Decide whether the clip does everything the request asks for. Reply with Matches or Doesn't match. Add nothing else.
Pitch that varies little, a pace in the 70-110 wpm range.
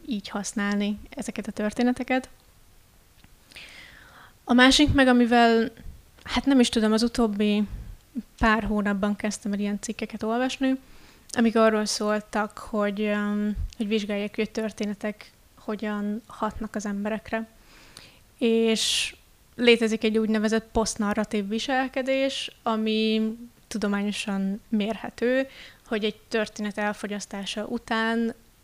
Matches